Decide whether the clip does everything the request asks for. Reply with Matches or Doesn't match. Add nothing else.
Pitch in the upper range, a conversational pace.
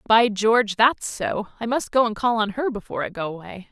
Doesn't match